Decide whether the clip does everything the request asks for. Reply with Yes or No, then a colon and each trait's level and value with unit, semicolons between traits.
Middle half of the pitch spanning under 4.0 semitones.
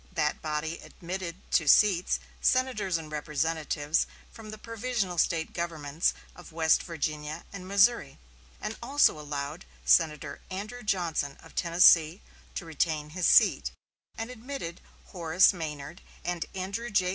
No: average, 4.4 semitones